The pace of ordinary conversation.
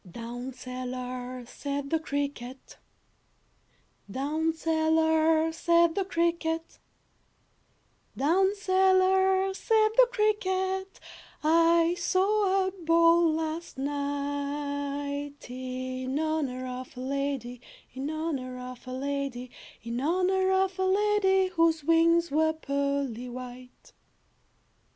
No: slow, 100 wpm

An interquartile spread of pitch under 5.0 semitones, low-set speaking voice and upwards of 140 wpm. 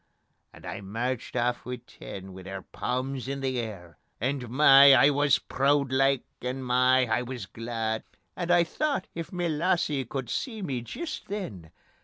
Yes: average, 3.4 semitones; low, 130 Hz; average, 170 wpm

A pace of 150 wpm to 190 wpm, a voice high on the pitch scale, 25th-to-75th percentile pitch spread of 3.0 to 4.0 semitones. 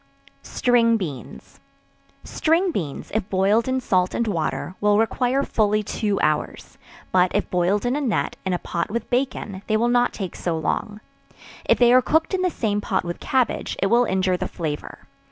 No: average, 185 wpm; high, 210 Hz; average, 4.8 semitones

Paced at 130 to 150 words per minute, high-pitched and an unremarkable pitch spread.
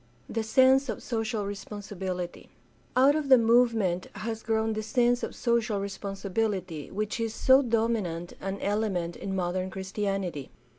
Yes: average, 145 wpm; high, 210 Hz; average, 3.3 semitones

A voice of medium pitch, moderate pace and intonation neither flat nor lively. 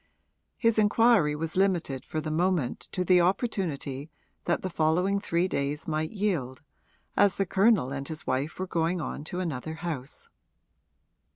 Yes: medium, 170 Hz; average, 155 wpm; average, 4.2 semitones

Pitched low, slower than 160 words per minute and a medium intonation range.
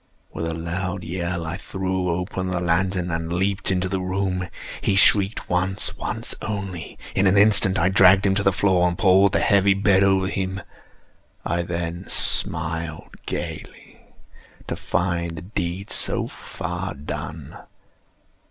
No: very low, 95 Hz; average, 145 wpm; narrow, 2.0 semitones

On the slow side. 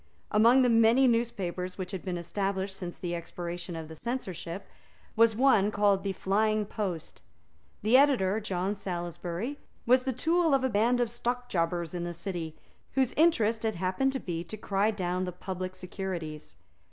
No: average, 165 wpm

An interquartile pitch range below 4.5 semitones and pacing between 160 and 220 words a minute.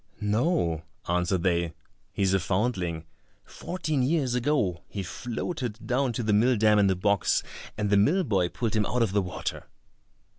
No: average, 5.1 semitones; average, 170 wpm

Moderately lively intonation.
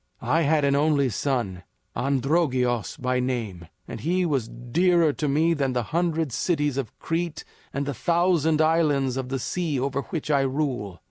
Yes: average, 4.1 semitones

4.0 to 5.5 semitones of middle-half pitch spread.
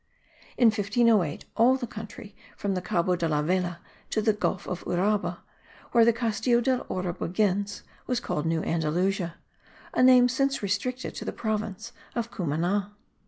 Yes: average, 4.7 semitones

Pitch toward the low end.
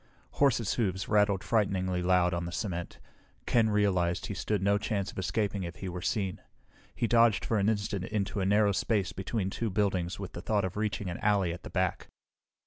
Yes: low, 100 Hz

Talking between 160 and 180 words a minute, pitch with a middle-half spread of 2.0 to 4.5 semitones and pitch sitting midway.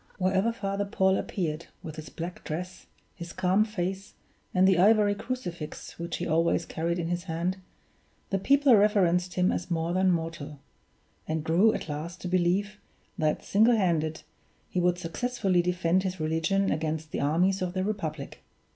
Yes: average, 165 wpm; average, 2.9 semitones; medium, 180 Hz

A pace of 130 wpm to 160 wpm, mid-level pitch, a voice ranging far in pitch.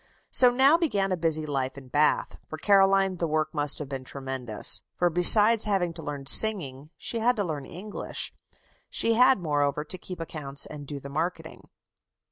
No: average, 180 wpm; medium, 165 Hz; wide, 5.7 semitones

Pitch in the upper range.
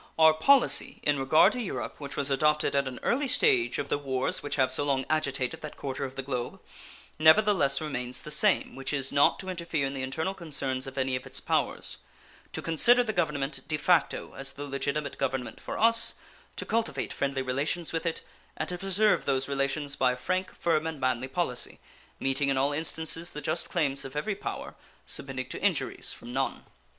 No: medium, 145 Hz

